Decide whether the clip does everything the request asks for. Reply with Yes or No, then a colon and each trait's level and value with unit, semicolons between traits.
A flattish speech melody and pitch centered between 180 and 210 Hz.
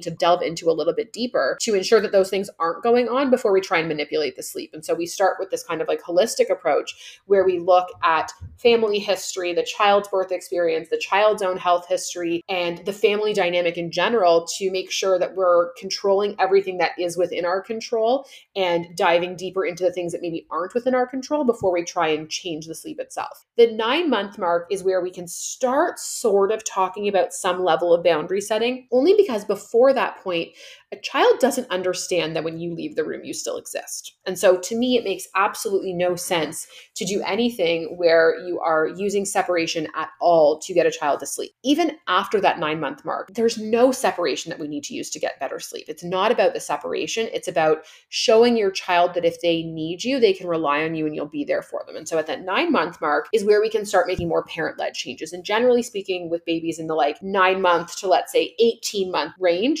No: average, 5.3 semitones; high, 190 Hz